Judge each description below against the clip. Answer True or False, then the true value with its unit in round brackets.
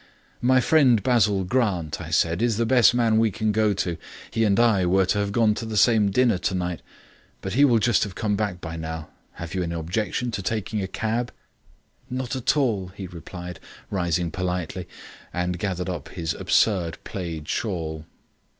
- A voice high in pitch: False (100 Hz)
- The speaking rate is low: False (185 wpm)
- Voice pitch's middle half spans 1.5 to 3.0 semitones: False (4.3 semitones)